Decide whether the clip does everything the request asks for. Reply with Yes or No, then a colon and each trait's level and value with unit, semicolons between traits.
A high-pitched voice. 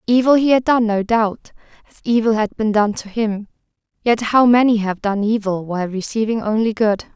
Yes: high, 220 Hz